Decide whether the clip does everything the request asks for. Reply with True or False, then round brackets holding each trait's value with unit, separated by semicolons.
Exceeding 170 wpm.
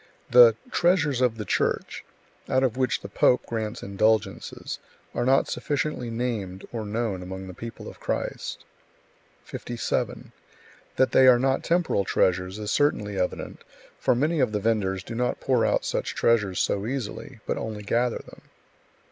False (155 wpm)